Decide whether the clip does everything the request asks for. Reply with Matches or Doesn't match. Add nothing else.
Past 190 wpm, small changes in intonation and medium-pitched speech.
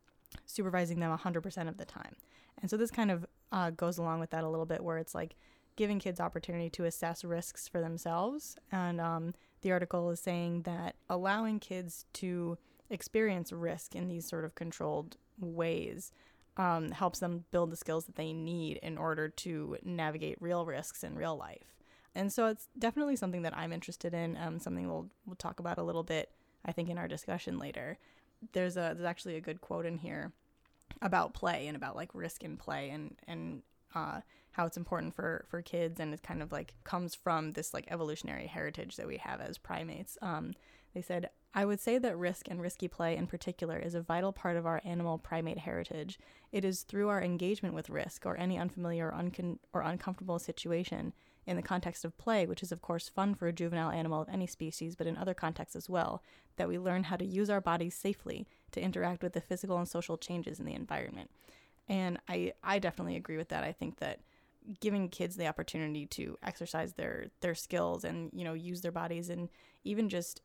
Matches